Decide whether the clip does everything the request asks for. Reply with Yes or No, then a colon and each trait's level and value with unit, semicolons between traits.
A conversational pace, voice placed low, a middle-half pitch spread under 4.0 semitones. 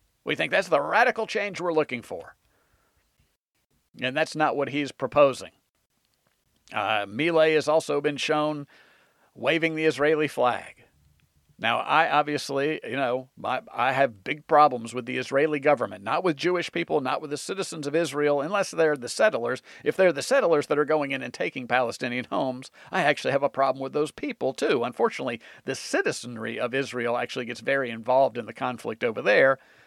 No: average, 175 wpm; medium, 145 Hz; average, 3.1 semitones